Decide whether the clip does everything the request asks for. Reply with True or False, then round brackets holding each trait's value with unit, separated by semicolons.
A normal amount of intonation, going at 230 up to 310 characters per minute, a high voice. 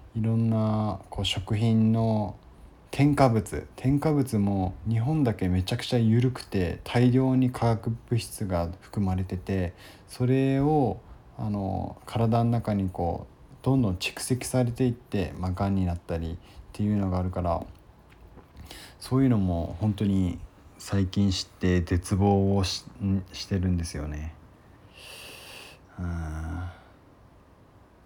False (4.1 semitones; 240 characters per minute; 100 Hz)